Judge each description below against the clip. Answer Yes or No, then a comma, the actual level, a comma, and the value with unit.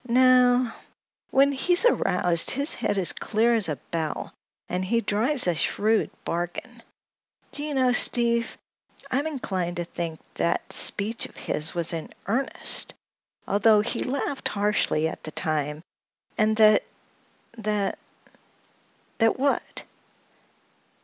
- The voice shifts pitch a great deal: Yes, wide, 6.2 semitones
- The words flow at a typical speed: No, slow, 125 wpm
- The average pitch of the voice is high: Yes, high, 215 Hz